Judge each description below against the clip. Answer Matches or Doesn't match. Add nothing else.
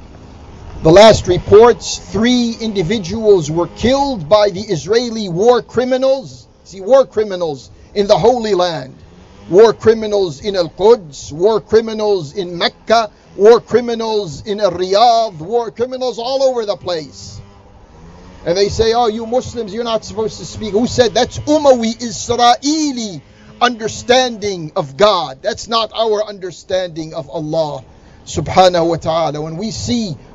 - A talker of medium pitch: Doesn't match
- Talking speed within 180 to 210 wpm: Doesn't match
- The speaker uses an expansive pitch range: Matches